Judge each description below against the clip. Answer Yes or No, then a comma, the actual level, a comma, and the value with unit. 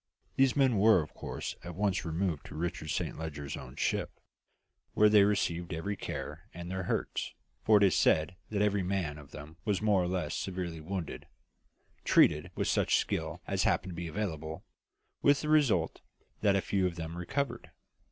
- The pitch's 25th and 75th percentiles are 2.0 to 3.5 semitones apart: No, average, 4.1 semitones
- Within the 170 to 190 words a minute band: Yes, average, 180 wpm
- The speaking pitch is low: Yes, very low, 90 Hz